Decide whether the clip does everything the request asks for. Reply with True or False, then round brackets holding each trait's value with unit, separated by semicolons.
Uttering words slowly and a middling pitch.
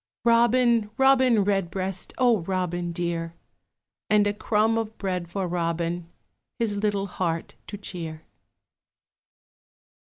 False (105 wpm; 195 Hz)